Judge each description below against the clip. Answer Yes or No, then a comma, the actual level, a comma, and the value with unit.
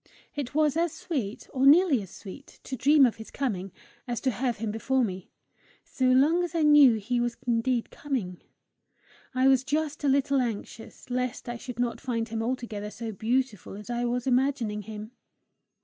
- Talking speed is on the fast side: No, average, 180 wpm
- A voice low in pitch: No, high, 245 Hz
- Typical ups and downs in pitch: Yes, average, 3.5 semitones